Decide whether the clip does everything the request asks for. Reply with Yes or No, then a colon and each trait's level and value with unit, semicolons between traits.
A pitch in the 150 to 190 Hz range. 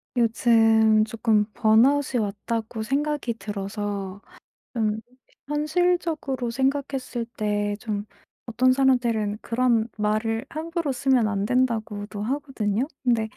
No: high, 230 Hz